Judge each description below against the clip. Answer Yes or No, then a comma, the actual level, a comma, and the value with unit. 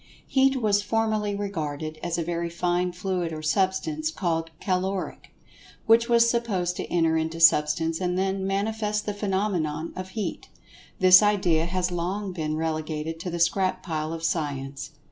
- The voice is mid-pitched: Yes, medium, 180 Hz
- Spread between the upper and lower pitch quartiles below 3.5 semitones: No, average, 3.8 semitones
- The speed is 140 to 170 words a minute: Yes, average, 160 wpm